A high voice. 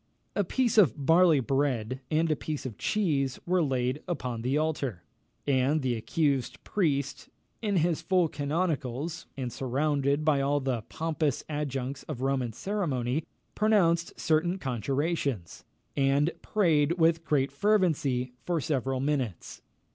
No: medium, 145 Hz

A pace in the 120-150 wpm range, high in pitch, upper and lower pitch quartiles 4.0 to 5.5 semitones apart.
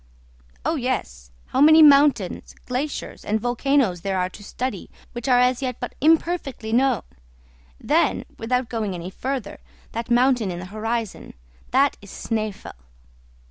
Yes: average, 140 wpm; high, 240 Hz; average, 4.6 semitones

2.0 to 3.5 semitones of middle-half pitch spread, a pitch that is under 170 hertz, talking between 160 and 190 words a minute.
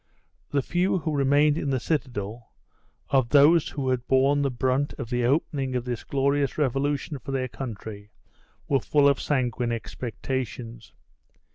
No: average, 2.9 semitones; low, 135 Hz; average, 150 wpm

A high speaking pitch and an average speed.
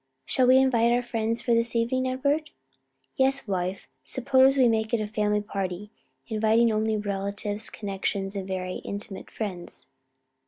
Yes: high, 220 Hz; average, 150 wpm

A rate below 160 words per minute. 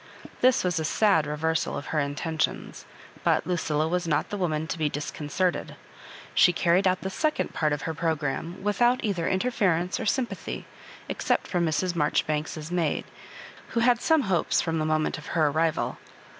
No: average, 170 wpm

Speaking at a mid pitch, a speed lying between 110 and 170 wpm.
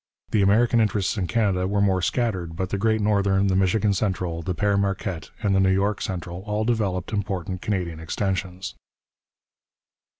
No: very low, 95 Hz; average, 165 wpm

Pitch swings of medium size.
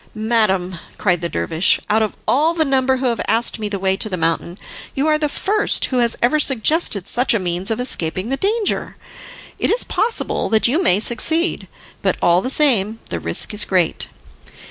No: wide, 6.5 semitones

